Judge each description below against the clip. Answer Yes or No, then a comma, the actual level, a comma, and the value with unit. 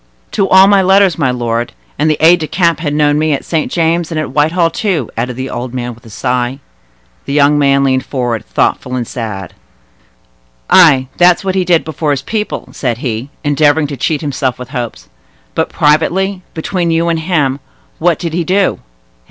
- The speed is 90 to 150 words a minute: No, average, 185 wpm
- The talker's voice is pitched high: No, medium, 150 Hz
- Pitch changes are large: No, average, 4.7 semitones